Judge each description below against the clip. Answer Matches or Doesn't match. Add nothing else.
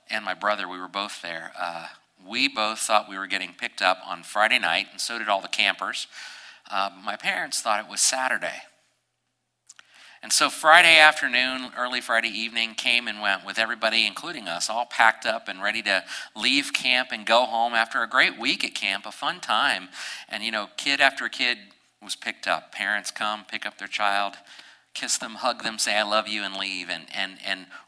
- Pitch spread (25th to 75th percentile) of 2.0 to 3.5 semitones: Matches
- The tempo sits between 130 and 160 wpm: Doesn't match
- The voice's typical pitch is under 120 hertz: Matches